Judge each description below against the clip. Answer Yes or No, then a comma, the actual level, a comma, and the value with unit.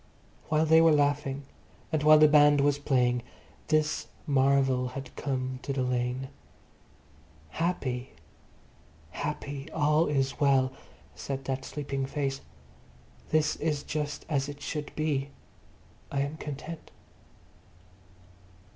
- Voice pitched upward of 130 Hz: Yes, medium, 140 Hz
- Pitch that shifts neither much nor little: No, narrow, 2.0 semitones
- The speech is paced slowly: Yes, slow, 115 wpm